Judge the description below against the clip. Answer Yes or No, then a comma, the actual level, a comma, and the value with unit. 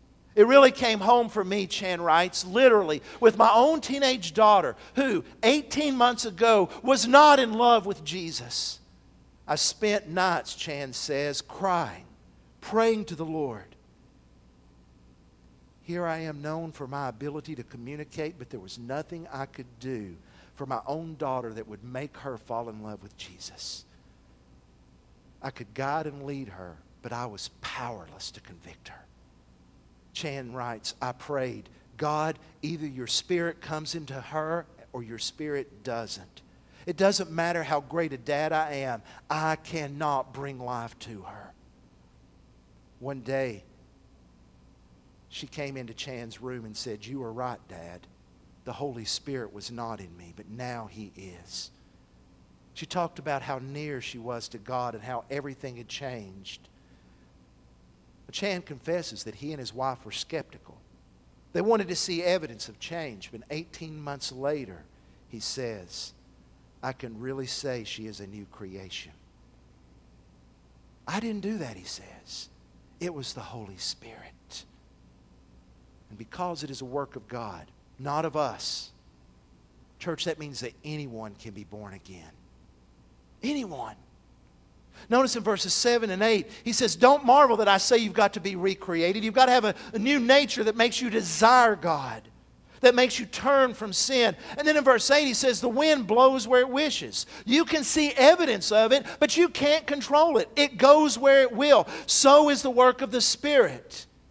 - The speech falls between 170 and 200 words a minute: No, average, 160 wpm